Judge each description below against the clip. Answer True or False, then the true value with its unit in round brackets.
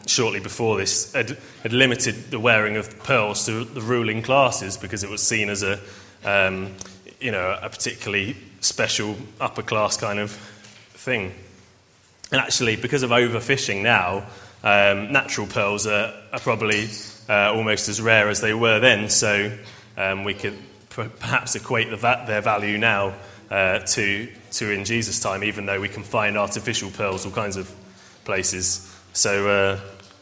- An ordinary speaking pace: True (160 wpm)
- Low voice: True (105 Hz)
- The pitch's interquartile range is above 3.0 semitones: False (2.5 semitones)